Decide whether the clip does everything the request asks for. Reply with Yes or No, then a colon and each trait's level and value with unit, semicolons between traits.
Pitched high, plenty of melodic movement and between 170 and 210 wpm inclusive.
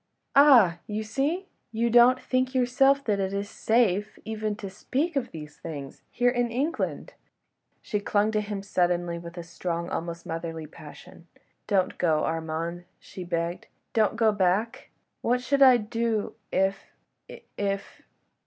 No: high, 205 Hz; wide, 5.8 semitones; average, 145 wpm